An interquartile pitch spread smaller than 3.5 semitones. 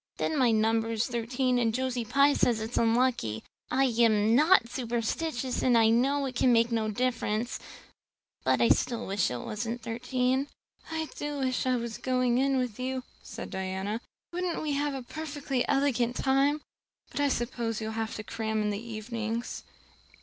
Yes: average, 2.9 semitones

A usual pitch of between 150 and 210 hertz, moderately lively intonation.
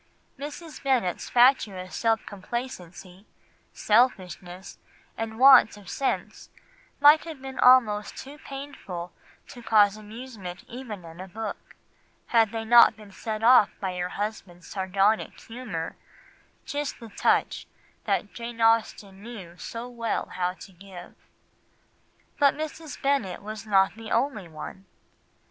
No: high, 220 Hz; average, 4.7 semitones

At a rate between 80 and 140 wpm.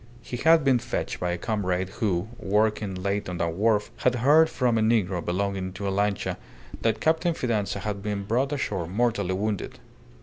No: average, 180 wpm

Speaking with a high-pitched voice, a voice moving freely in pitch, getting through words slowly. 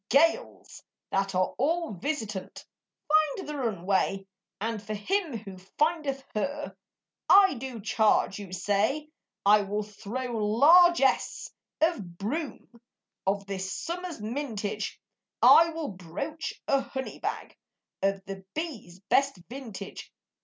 Yes: high, 225 Hz; wide, 7.1 semitones; slow, 115 wpm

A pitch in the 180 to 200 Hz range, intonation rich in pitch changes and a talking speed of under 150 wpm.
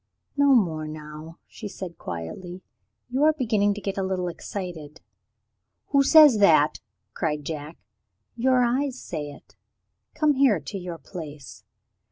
Yes: medium, 185 Hz; wide, 8.0 semitones; average, 140 wpm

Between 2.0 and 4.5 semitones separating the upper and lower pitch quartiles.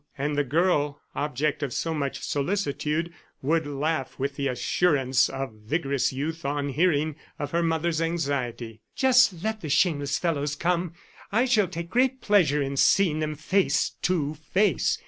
Yes: average, 3.6 semitones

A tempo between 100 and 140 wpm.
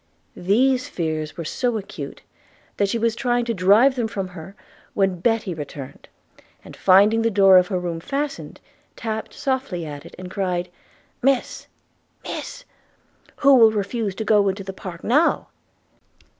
No: average, 155 wpm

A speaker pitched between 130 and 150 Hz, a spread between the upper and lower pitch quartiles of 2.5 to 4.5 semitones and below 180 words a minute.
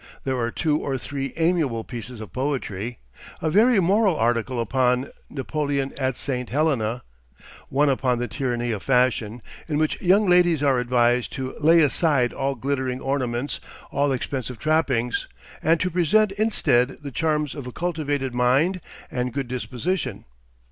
Yes: low, 135 Hz; average, 4.0 semitones; average, 150 wpm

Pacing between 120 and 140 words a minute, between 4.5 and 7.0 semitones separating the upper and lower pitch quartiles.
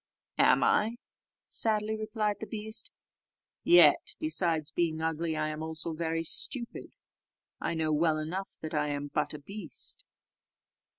Yes: slow, 135 wpm; wide, 5.4 semitones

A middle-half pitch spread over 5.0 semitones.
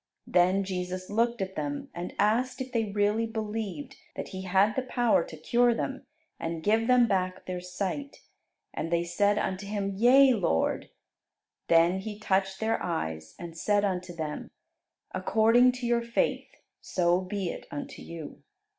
No: average, 4.2 semitones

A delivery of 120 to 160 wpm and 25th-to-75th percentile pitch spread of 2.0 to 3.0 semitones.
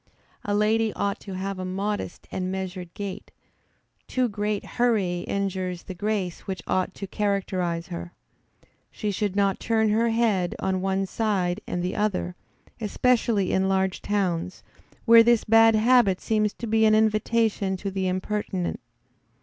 Yes: average, 150 wpm; narrow, 2.6 semitones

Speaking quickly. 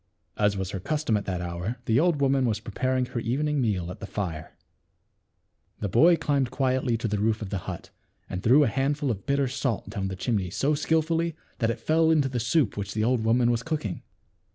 Yes: fast, 215 wpm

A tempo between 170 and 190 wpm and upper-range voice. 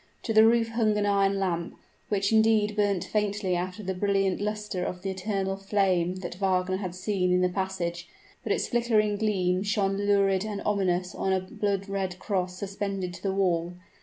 Yes: average, 185 wpm; high, 195 Hz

